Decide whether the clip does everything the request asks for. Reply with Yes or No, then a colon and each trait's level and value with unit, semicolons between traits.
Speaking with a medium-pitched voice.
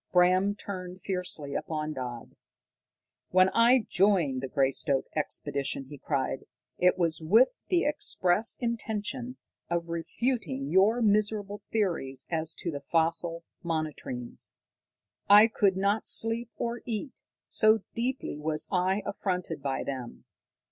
Yes: medium, 180 Hz